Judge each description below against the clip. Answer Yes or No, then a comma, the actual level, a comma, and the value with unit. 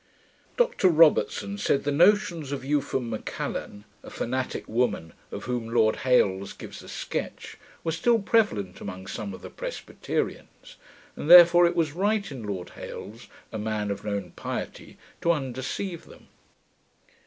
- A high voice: No, low, 130 Hz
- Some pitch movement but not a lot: No, wide, 8.4 semitones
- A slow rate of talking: No, average, 145 wpm